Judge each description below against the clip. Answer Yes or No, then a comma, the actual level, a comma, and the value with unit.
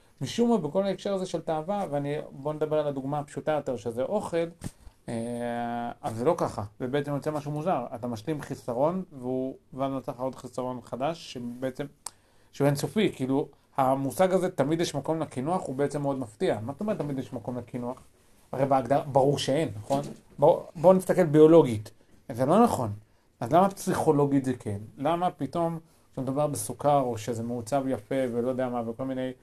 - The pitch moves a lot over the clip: No, average, 3.8 semitones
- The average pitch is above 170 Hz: No, medium, 140 Hz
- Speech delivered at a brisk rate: Yes, fast, 175 wpm